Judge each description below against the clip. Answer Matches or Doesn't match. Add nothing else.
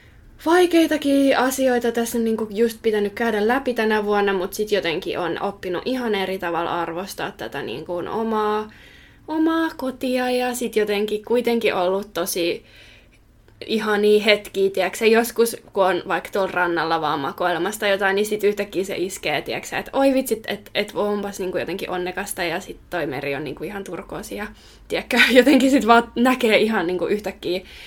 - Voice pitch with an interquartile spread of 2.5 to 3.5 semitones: Doesn't match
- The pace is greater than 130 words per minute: Matches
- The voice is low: Doesn't match